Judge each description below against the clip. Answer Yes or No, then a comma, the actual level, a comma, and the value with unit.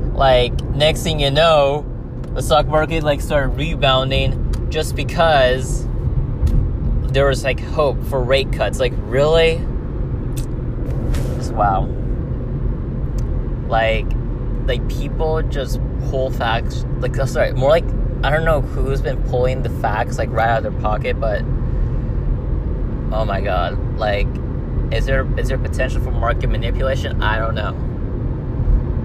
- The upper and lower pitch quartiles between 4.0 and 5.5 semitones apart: No, narrow, 2.4 semitones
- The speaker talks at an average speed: No, slow, 130 wpm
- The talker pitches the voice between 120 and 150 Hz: Yes, low, 130 Hz